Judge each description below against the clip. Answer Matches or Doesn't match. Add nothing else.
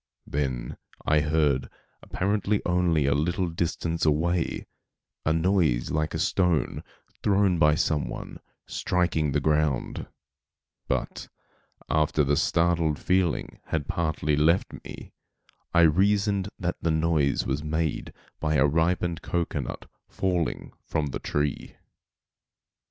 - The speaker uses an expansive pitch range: Doesn't match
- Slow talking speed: Matches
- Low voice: Matches